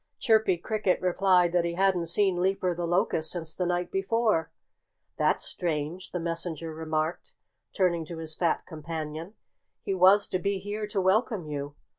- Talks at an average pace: Yes, average, 160 wpm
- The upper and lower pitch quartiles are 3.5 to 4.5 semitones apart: No, average, 2.9 semitones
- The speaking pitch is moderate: Yes, medium, 180 Hz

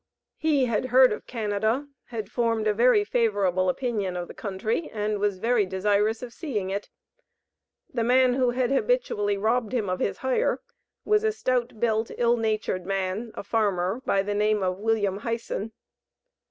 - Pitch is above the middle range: Yes, high, 220 Hz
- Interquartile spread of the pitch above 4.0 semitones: No, average, 3.3 semitones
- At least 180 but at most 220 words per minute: No, average, 165 wpm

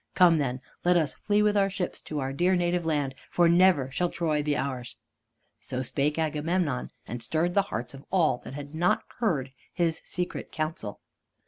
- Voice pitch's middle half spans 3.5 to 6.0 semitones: Yes, average, 4.3 semitones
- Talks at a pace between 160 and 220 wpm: Yes, average, 185 wpm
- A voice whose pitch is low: No, medium, 160 Hz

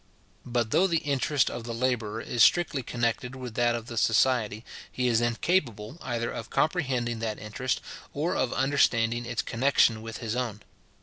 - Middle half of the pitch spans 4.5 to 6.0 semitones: No, narrow, 2.5 semitones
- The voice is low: Yes, low, 120 Hz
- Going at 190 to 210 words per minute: No, average, 170 wpm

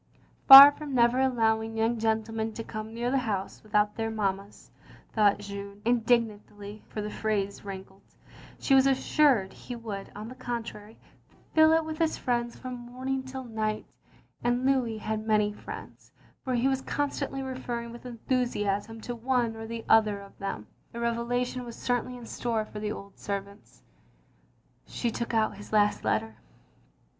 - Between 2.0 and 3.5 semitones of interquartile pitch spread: Yes, average, 2.9 semitones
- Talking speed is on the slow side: No, average, 165 wpm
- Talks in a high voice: Yes, high, 225 Hz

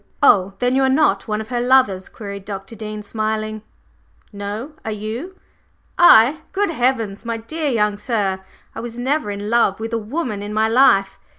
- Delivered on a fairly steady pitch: No, average, 3.6 semitones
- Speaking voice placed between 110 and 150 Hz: No, high, 220 Hz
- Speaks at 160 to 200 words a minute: Yes, average, 180 wpm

